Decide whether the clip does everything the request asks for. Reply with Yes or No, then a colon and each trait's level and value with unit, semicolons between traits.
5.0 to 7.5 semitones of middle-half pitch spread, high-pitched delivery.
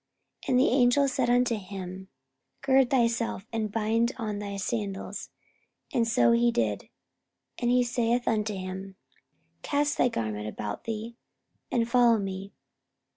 No: average, 4.2 semitones; high, 225 Hz